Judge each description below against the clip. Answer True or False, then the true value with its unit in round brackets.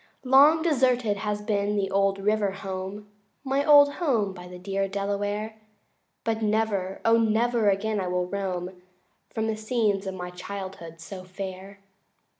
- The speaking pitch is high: True (205 Hz)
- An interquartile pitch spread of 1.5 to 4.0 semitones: True (2.5 semitones)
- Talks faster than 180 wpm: False (155 wpm)